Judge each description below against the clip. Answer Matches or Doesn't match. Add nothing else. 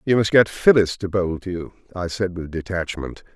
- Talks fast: Matches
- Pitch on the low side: Matches